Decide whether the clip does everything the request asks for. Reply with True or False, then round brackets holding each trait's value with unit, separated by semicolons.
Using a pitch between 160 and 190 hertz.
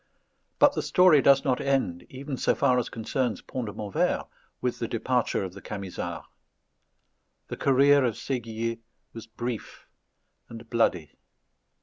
False (120 Hz)